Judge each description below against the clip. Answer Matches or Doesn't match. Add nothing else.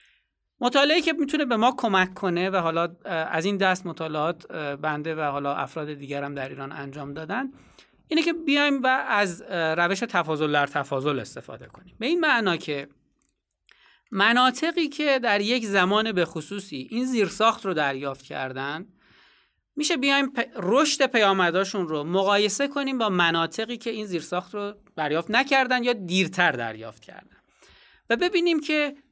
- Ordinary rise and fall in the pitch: Doesn't match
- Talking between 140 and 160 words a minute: Matches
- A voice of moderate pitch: Doesn't match